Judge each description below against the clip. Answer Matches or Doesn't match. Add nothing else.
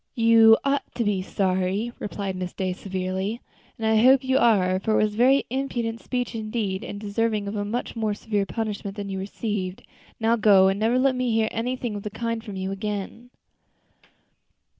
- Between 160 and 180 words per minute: Doesn't match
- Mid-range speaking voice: Doesn't match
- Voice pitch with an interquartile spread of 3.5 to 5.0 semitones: Doesn't match